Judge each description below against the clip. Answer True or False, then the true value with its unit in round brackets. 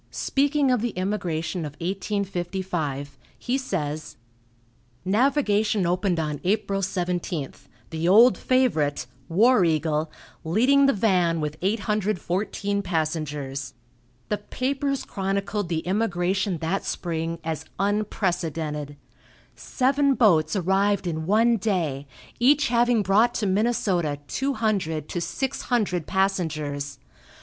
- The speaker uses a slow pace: True (110 wpm)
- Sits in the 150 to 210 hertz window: True (190 Hz)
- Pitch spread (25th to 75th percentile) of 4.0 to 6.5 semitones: True (5.0 semitones)